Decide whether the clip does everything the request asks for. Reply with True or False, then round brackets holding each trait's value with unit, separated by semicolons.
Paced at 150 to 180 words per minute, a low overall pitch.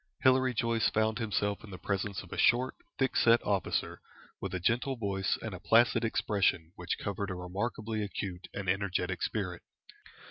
True (170 wpm; 100 Hz)